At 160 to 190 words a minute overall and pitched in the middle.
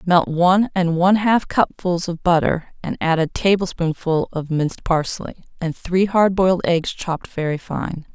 Yes: average, 170 wpm; medium, 175 Hz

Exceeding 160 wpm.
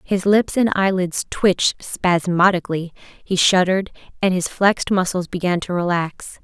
No: average, 140 wpm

